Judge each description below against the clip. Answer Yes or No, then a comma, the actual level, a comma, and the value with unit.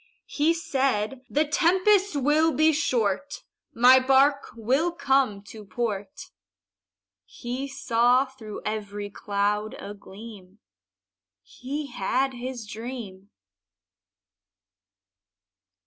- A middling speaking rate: No, slow, 90 wpm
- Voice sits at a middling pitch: No, very high, 255 Hz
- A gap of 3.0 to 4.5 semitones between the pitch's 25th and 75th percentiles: No, average, 5.2 semitones